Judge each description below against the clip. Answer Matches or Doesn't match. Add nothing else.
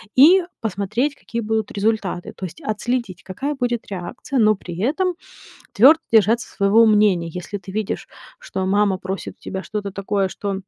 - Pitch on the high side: Matches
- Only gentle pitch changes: Doesn't match